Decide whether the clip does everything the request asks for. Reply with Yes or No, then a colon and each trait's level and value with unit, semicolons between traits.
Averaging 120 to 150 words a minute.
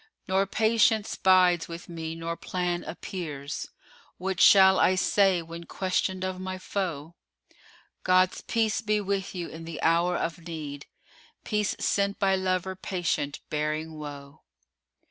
Yes: average, 145 wpm